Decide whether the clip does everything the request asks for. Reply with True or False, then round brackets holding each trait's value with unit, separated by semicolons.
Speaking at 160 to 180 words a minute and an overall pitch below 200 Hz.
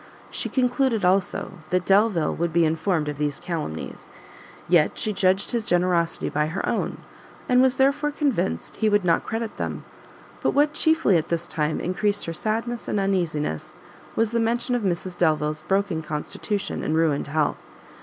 True (165 wpm; 185 Hz)